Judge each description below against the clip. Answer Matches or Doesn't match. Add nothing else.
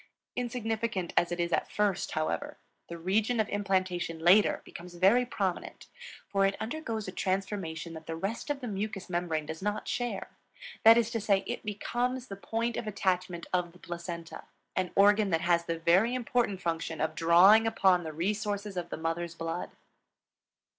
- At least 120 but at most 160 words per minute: Doesn't match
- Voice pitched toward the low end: Doesn't match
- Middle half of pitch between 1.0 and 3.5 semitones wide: Doesn't match